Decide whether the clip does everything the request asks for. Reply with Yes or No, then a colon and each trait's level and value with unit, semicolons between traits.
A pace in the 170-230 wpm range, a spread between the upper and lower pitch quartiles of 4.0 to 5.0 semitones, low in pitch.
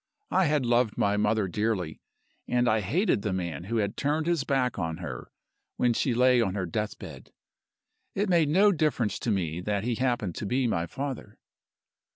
No: average, 185 wpm; wide, 5.4 semitones; low, 115 Hz